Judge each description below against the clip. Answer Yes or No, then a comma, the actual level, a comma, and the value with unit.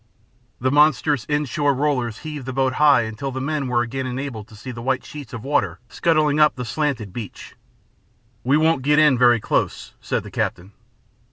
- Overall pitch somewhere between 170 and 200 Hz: No, low, 135 Hz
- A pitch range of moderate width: Yes, average, 3.6 semitones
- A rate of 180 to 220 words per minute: Yes, average, 190 wpm